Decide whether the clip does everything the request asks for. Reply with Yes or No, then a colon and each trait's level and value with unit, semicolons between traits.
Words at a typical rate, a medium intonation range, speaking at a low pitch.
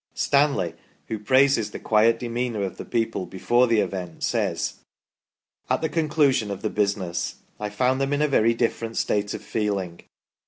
Yes: average, 170 wpm; average, 4.3 semitones; low, 115 Hz